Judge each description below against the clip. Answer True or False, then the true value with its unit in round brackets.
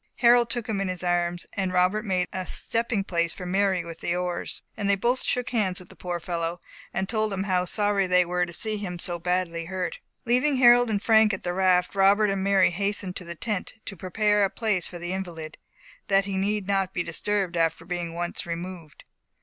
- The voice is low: False (190 Hz)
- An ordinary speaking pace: False (215 wpm)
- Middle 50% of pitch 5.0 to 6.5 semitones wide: False (2.8 semitones)